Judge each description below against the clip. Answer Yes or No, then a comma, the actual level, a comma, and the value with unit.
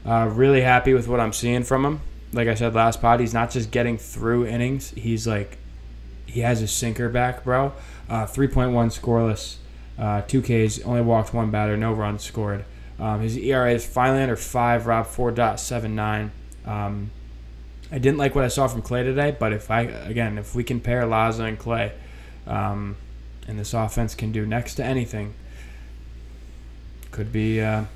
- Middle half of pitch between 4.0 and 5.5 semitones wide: No, average, 2.9 semitones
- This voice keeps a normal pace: Yes, average, 175 wpm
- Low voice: Yes, low, 115 Hz